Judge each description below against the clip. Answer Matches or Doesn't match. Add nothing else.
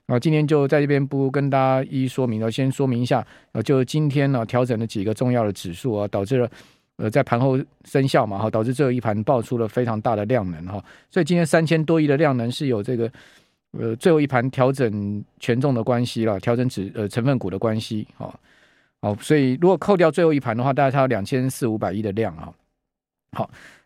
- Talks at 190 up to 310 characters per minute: Doesn't match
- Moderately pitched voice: Doesn't match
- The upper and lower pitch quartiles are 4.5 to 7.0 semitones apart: Doesn't match